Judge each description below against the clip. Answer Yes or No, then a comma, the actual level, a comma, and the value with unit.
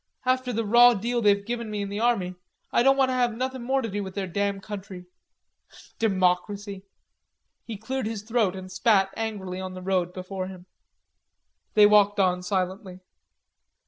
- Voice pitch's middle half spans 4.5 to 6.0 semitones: No, average, 3.6 semitones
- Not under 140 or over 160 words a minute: No, average, 175 wpm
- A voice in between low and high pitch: No, high, 205 Hz